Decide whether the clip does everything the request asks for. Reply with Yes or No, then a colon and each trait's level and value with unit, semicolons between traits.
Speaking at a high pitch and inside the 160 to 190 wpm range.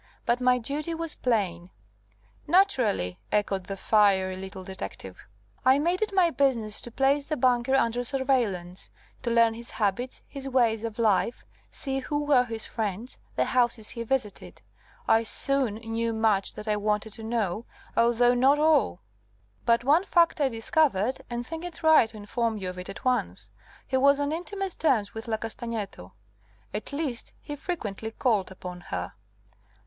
Yes: high, 235 Hz; average, 165 wpm